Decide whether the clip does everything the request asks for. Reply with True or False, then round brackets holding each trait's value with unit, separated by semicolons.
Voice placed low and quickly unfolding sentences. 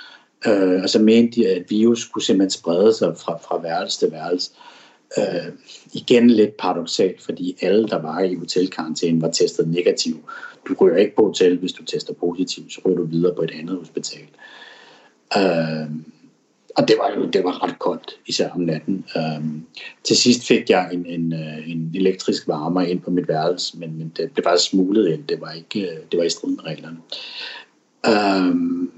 False (95 Hz; 190 wpm)